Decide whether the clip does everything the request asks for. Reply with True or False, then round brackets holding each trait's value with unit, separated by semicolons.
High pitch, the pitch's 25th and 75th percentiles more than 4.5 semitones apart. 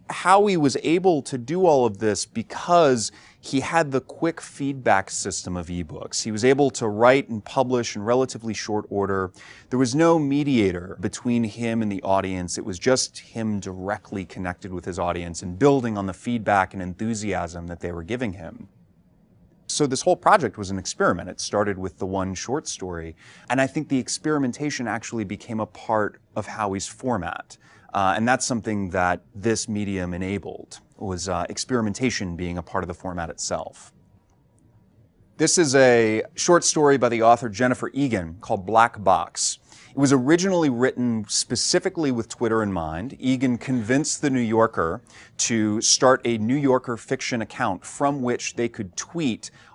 False (115 Hz; 5.1 semitones)